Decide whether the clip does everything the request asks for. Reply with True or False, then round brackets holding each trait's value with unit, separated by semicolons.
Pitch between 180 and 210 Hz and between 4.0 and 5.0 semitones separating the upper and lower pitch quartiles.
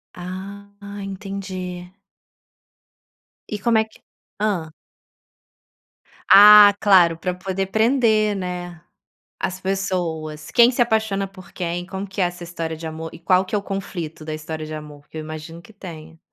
False (185 Hz; 3.5 semitones)